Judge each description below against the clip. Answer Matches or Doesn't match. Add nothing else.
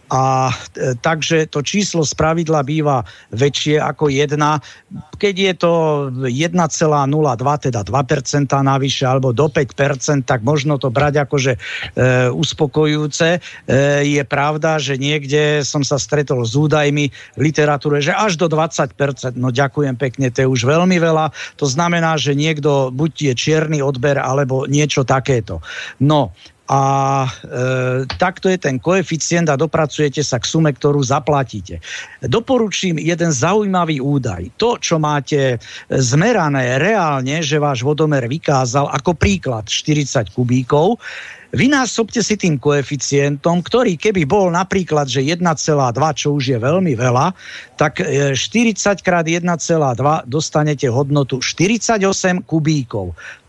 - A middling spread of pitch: Matches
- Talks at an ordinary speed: Matches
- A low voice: Doesn't match